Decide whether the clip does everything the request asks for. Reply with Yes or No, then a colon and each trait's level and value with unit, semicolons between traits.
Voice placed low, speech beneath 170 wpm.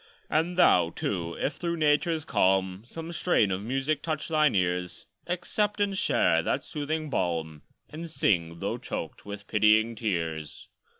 Yes: low, 115 Hz; average, 145 wpm